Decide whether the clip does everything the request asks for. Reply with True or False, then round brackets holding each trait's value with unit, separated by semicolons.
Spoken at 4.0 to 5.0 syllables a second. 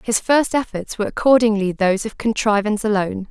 False (6.2 syllables/s)